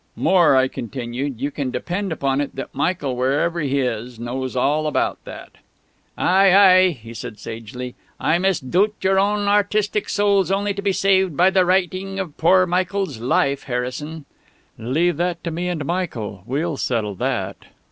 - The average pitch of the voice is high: No, medium, 160 Hz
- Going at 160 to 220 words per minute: Yes, average, 165 wpm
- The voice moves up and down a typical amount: No, wide, 6.6 semitones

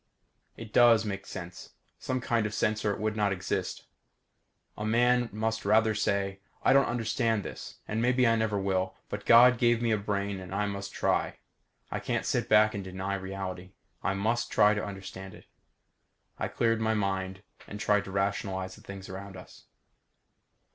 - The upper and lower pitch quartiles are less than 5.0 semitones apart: Yes, narrow, 2.4 semitones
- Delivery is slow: No, average, 180 wpm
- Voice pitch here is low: Yes, low, 105 Hz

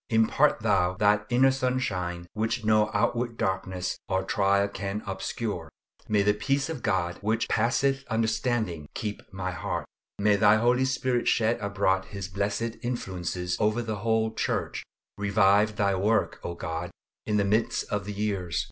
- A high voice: No, low, 105 Hz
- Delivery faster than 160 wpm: No, average, 155 wpm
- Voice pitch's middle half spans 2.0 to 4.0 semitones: Yes, average, 3.0 semitones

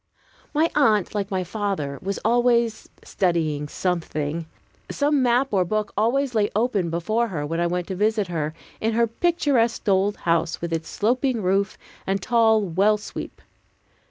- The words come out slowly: No, average, 155 wpm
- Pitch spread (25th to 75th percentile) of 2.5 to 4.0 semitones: No, average, 5.2 semitones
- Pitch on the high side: Yes, high, 205 Hz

